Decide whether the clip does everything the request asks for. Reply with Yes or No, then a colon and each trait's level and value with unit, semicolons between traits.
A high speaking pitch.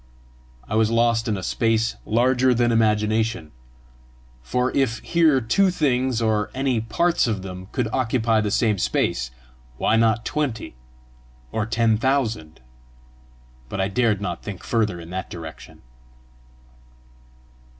No: low, 115 Hz